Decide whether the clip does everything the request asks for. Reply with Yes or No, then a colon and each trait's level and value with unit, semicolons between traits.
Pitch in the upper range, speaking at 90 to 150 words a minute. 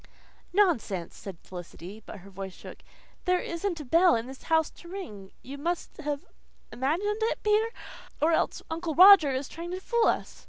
No: very high, 320 Hz; average, 175 wpm